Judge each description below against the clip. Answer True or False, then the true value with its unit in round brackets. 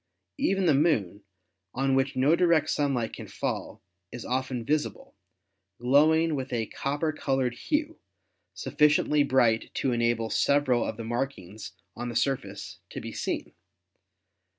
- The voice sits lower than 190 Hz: True (135 Hz)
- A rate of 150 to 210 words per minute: False (135 wpm)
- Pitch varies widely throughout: False (4.0 semitones)